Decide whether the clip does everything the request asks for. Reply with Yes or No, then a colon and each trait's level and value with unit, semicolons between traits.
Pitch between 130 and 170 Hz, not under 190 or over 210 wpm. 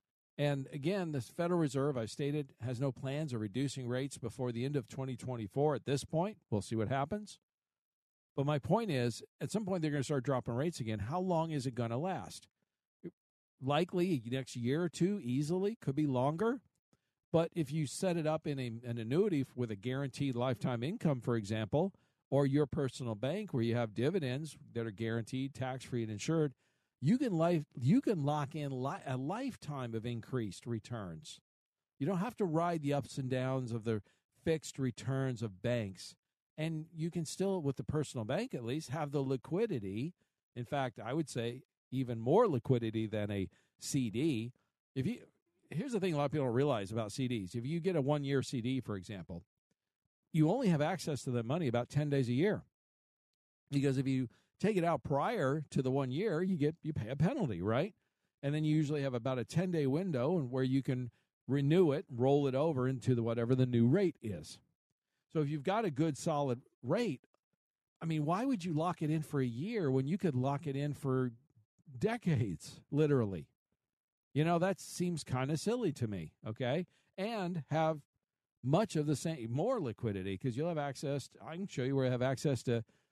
Yes: medium, 140 Hz; average, 200 wpm